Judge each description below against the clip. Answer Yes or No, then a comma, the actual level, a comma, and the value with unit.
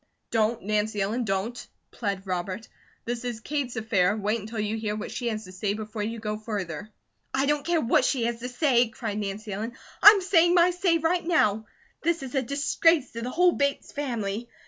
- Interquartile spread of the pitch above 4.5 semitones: Yes, average, 4.9 semitones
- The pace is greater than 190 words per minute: Yes, average, 200 wpm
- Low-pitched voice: No, high, 230 Hz